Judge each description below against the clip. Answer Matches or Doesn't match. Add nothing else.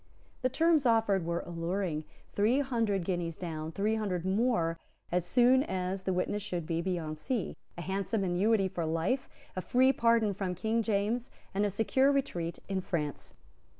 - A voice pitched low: Doesn't match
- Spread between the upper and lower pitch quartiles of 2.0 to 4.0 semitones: Doesn't match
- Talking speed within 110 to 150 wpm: Doesn't match